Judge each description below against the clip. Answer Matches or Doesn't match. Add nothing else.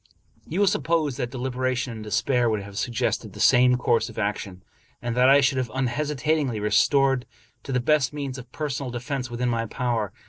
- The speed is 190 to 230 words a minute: Matches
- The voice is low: Matches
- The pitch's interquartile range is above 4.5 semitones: Doesn't match